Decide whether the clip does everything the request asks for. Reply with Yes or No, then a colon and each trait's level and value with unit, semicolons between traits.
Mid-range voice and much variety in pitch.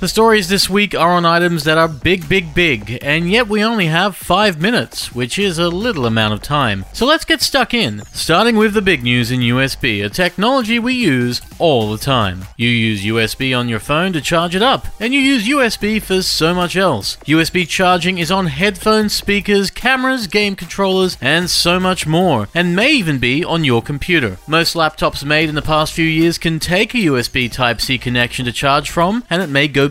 Yes: medium, 170 Hz; wide, 6.9 semitones